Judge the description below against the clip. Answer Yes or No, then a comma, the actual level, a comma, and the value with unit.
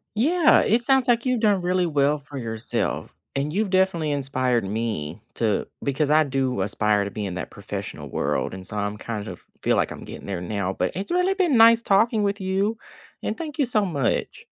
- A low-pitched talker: No, medium, 150 Hz